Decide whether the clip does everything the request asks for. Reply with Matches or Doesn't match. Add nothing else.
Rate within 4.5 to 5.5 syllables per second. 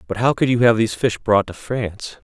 Doesn't match